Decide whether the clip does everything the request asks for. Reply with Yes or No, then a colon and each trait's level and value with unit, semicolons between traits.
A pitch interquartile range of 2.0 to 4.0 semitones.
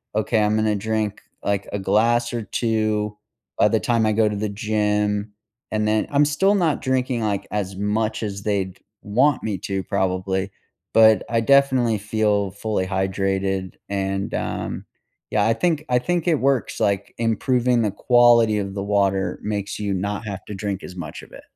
Yes: average, 2.8 semitones